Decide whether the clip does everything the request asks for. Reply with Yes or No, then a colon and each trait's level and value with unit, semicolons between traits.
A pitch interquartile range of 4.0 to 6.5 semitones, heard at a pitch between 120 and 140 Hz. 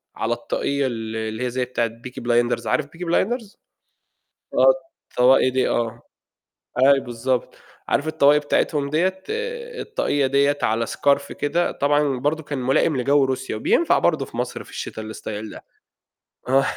No: average, 3.6 semitones; low, 135 Hz